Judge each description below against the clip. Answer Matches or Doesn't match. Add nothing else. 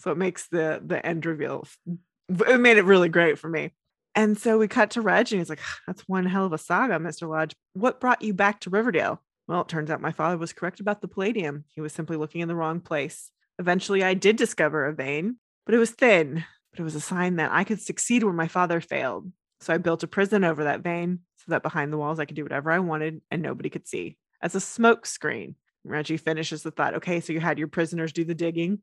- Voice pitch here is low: Doesn't match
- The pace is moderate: Doesn't match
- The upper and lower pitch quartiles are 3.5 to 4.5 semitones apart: Matches